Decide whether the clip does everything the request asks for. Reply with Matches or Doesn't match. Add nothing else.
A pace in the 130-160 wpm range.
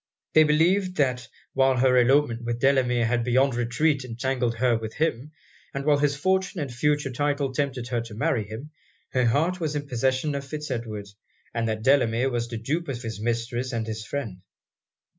Doesn't match